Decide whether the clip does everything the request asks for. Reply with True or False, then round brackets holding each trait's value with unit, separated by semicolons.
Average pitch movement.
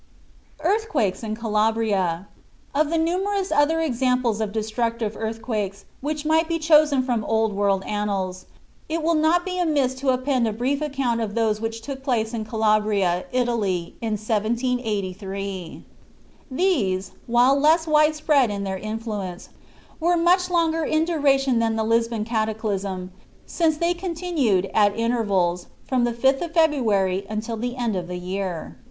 False (6.3 semitones)